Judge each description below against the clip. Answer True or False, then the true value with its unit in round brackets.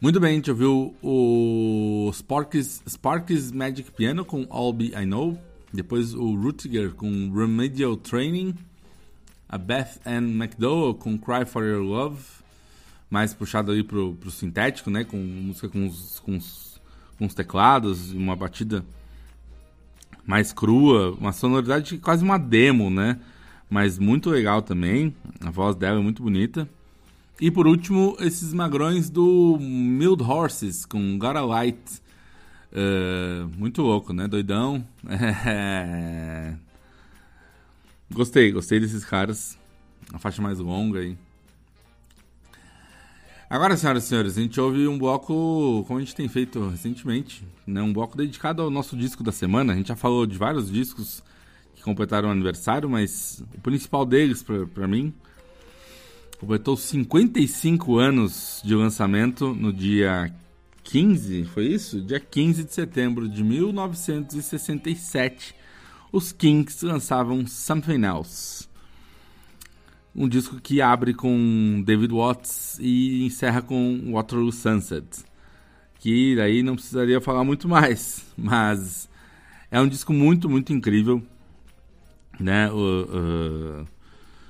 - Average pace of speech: True (130 wpm)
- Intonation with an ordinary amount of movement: False (5.7 semitones)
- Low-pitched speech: True (115 Hz)